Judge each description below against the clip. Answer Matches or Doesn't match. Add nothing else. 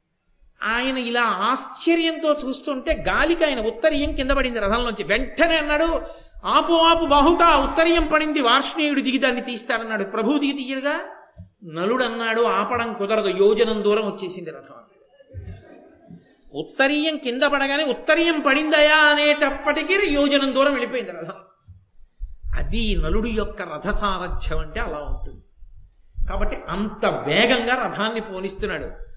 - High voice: Matches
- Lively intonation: Matches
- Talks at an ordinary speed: Matches